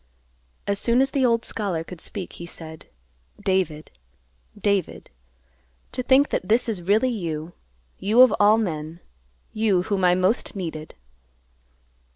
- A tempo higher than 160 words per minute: No, average, 140 wpm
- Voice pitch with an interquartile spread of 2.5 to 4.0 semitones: No, average, 4.7 semitones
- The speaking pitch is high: Yes, high, 195 Hz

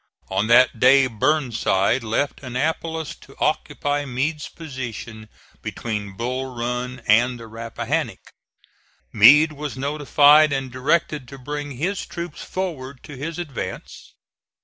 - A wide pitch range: No, average, 3.8 semitones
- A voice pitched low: Yes, low, 130 Hz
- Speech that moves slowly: Yes, slow, 120 wpm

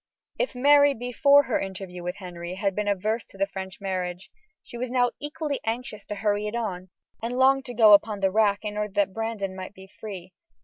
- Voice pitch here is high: Yes, high, 210 Hz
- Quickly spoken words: Yes, fast, 210 wpm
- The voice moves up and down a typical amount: Yes, average, 4.1 semitones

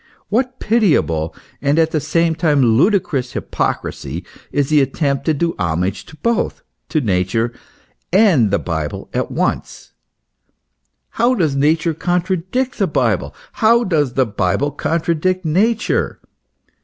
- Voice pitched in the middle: Yes, medium, 155 Hz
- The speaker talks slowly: Yes, slow, 130 wpm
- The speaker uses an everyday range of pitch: No, wide, 6.7 semitones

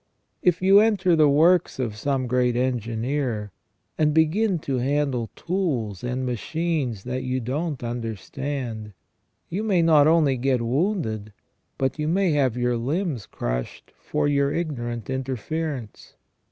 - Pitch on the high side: No, low, 135 Hz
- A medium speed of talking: No, slow, 130 wpm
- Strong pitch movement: No, average, 5.0 semitones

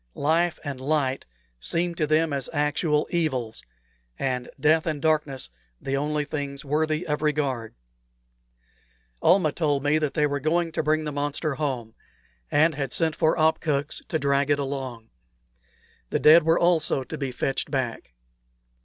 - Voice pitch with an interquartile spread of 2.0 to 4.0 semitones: Yes, narrow, 2.4 semitones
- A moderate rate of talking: Yes, average, 155 wpm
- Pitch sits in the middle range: Yes, medium, 150 Hz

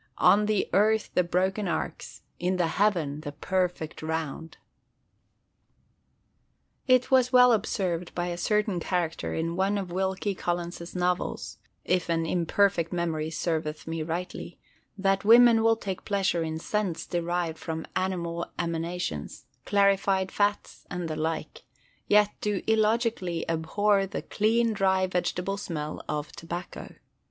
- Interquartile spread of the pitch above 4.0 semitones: No, average, 3.4 semitones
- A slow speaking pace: Yes, slow, 130 wpm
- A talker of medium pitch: Yes, medium, 180 Hz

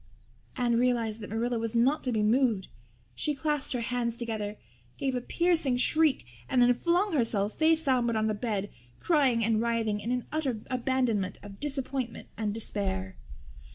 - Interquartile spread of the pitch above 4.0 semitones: No, average, 3.5 semitones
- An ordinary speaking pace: Yes, average, 165 wpm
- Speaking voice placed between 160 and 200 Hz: No, high, 240 Hz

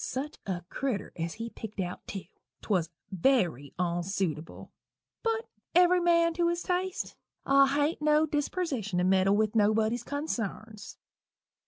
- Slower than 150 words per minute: Yes, slow, 135 wpm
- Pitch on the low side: No, high, 230 Hz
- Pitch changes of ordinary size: No, wide, 8.3 semitones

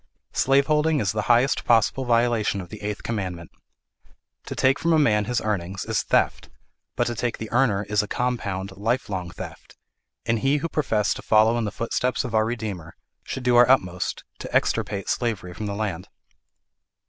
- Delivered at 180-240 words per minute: Yes, average, 185 wpm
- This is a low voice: Yes, low, 110 Hz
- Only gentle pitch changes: No, average, 3.6 semitones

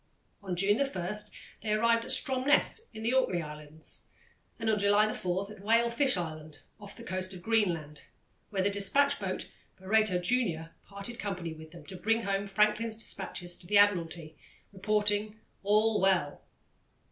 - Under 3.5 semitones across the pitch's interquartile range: No, average, 3.9 semitones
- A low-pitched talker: No, high, 200 Hz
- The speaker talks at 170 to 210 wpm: No, average, 160 wpm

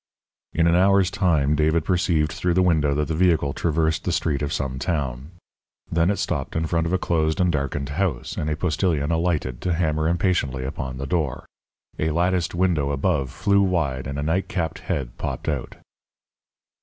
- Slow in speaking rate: No, average, 180 wpm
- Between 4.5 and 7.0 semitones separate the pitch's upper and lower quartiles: No, average, 3.7 semitones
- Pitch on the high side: No, very low, 80 Hz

